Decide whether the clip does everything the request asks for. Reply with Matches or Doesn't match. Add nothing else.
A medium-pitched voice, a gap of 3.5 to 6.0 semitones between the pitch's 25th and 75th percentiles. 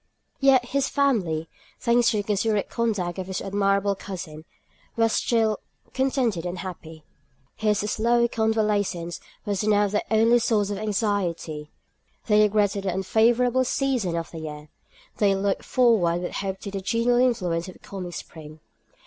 Doesn't match